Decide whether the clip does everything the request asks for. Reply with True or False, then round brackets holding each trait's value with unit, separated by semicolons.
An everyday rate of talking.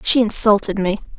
True (150 wpm)